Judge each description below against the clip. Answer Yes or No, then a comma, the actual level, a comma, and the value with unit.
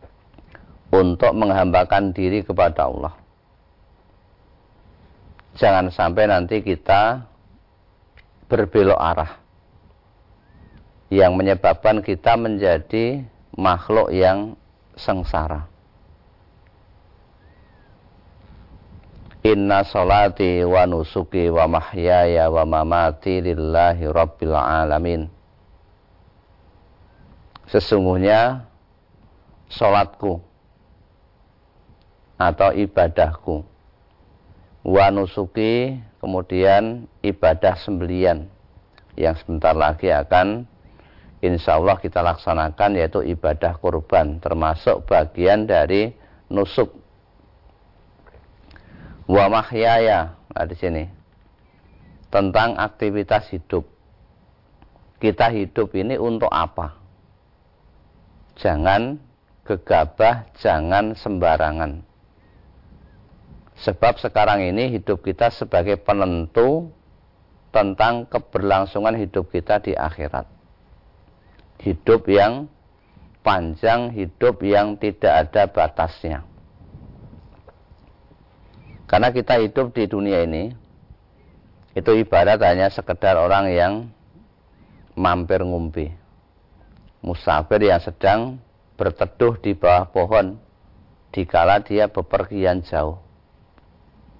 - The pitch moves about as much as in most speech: Yes, average, 3.6 semitones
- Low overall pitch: Yes, very low, 95 Hz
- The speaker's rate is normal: No, slow, 70 wpm